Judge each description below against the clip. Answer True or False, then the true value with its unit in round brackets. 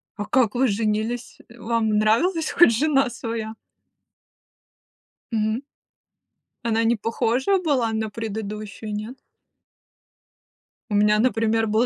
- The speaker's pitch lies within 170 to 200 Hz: False (225 Hz)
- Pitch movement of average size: False (2.1 semitones)